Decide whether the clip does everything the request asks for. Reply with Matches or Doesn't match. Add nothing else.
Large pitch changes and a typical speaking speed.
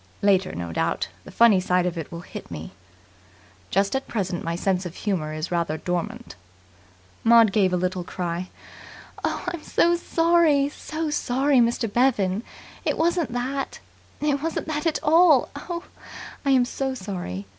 Matches